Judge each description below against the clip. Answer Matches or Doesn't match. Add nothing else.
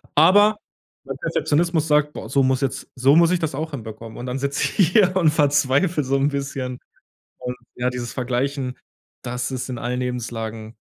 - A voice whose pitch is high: Doesn't match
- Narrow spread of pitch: Doesn't match